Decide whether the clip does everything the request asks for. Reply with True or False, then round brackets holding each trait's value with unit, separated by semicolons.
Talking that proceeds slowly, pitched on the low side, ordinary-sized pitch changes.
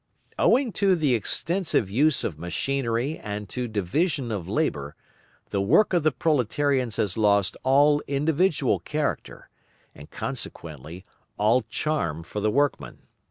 False (130 wpm; 130 Hz; 7.0 semitones)